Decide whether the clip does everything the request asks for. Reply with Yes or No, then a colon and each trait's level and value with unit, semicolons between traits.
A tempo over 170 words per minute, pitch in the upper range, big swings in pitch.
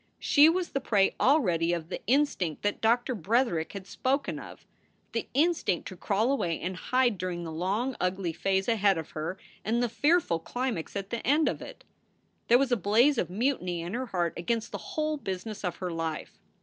Yes: average, 195 wpm; high, 205 Hz; wide, 6.4 semitones